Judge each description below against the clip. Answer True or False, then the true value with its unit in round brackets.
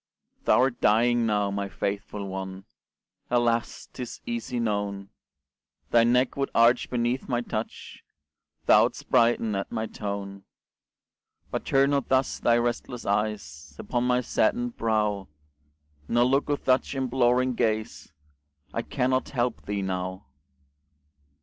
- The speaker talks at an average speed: False (125 wpm)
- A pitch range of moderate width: True (3.6 semitones)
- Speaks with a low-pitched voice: True (115 Hz)